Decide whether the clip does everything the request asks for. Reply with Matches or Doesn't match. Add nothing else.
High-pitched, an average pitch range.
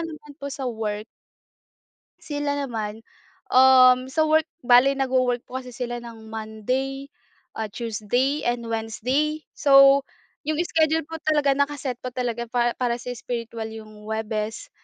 Matches